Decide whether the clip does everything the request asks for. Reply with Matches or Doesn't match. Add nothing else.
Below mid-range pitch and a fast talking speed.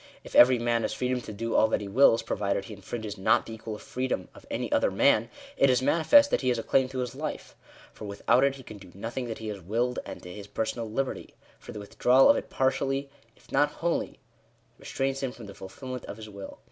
Matches